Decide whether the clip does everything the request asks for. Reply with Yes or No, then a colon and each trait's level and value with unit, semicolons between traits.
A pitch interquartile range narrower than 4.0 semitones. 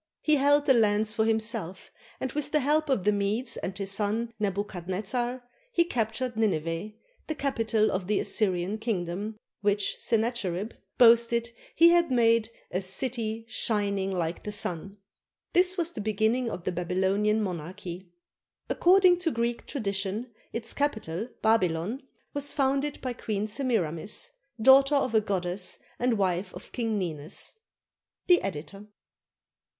No: average, 4.4 semitones